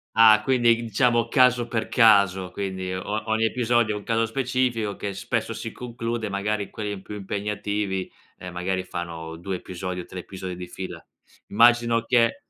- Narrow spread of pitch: No, average, 3.7 semitones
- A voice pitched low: Yes, low, 105 Hz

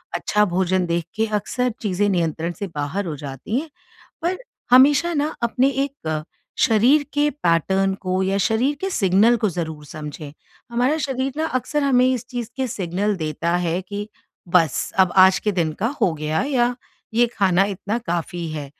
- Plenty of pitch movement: Yes, wide, 6.4 semitones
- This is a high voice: Yes, high, 195 Hz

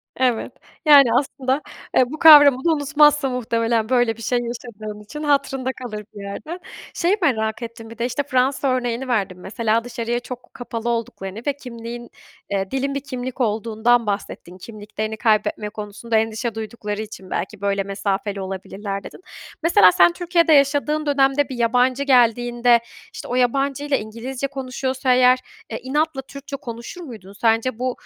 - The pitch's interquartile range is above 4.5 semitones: No, average, 3.7 semitones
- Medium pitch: No, high, 240 Hz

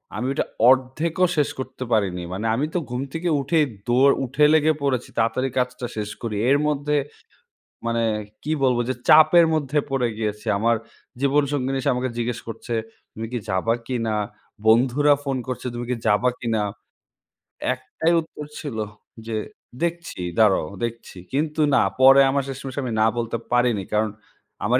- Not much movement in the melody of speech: No, average, 3.8 semitones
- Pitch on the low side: Yes, low, 125 Hz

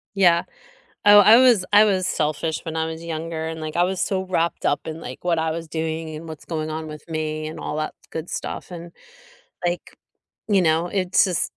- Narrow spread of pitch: Yes, narrow, 2.3 semitones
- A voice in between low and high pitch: Yes, medium, 165 Hz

